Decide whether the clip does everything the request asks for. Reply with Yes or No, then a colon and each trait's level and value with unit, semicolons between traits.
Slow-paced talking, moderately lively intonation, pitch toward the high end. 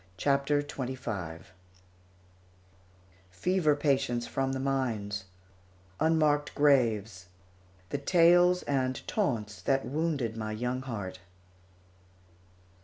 No: slow, 85 wpm; average, 4.7 semitones; low, 135 Hz